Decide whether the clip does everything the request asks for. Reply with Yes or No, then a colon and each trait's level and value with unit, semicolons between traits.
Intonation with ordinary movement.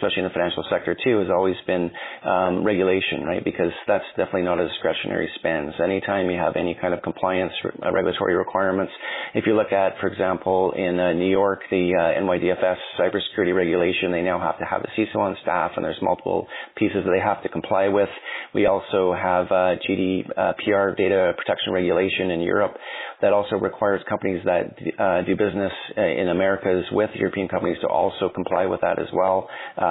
No: narrow, 1.2 semitones